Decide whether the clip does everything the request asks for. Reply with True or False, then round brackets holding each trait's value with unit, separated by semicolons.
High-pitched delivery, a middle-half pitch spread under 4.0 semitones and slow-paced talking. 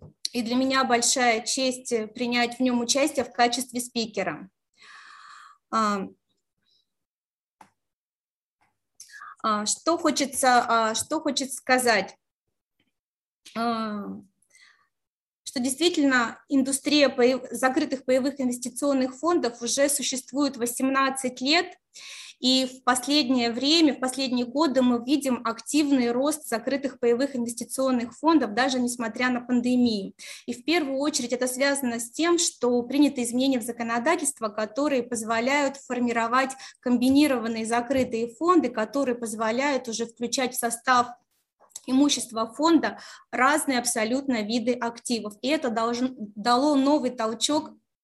True (255 Hz; 2.8 semitones; 105 wpm)